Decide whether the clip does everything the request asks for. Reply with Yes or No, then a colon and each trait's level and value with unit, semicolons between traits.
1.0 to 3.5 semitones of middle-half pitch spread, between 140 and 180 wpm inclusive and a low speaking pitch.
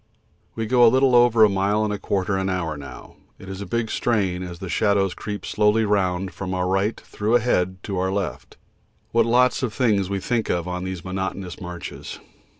No: average, 3.1 semitones; average, 200 wpm; low, 100 Hz